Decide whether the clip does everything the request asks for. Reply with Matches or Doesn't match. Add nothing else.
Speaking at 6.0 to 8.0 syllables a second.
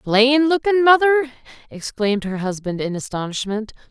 Doesn't match